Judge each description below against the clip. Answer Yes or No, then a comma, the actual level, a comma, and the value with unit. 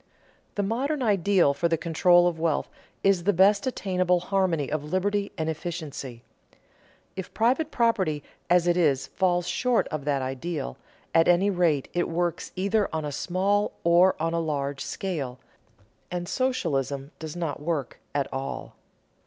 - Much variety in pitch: No, average, 4.2 semitones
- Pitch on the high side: No, medium, 175 Hz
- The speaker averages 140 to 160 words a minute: Yes, average, 155 wpm